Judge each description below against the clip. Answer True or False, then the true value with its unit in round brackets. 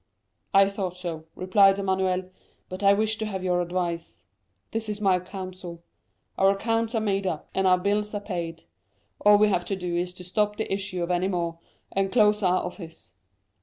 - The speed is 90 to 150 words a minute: False (180 wpm)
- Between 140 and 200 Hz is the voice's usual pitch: True (190 Hz)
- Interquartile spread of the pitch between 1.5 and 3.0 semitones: True (2.4 semitones)